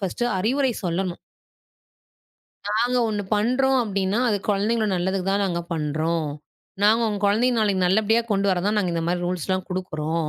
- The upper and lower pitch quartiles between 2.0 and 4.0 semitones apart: Yes, average, 3.5 semitones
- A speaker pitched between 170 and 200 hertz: Yes, high, 195 Hz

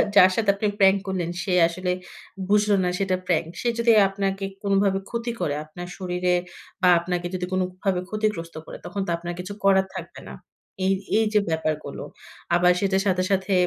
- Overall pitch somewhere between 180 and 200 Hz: Yes, high, 190 Hz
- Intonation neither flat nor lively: No, narrow, 1.9 semitones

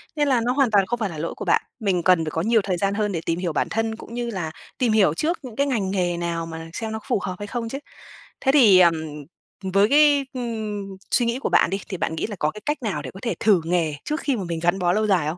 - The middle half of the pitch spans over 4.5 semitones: Yes, average, 5.2 semitones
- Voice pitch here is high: Yes, high, 205 Hz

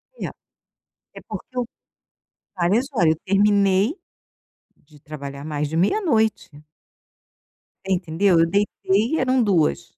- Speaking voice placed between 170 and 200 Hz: Yes, high, 190 Hz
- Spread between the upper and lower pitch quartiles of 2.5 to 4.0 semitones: No, wide, 5.4 semitones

